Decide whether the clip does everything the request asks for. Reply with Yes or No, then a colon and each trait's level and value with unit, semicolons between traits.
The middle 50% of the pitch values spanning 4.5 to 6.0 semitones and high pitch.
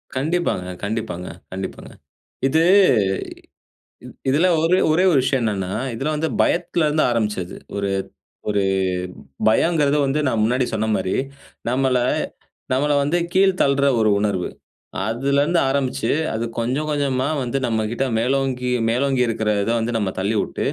No: average, 4.8 semitones; low, 130 Hz